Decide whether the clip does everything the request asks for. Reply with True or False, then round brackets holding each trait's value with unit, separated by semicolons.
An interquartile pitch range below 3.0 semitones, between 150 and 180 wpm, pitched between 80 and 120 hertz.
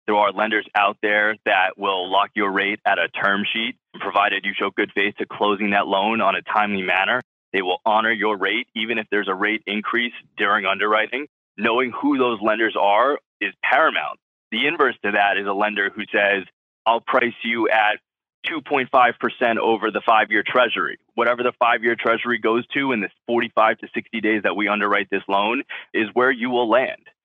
False (2.4 semitones; 195 wpm; 110 Hz)